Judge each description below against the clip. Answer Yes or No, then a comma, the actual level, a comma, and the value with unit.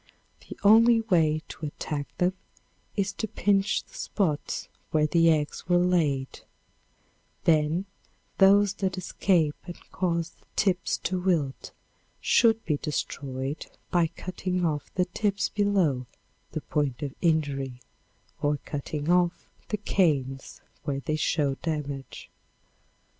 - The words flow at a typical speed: No, slow, 125 wpm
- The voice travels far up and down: No, average, 4.2 semitones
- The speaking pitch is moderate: Yes, medium, 165 Hz